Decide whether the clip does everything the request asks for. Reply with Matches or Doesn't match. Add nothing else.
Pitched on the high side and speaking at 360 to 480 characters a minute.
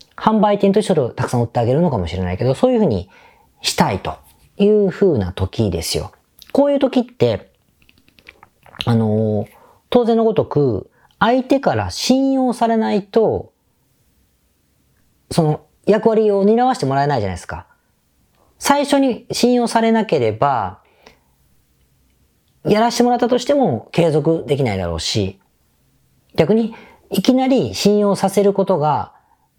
Doesn't match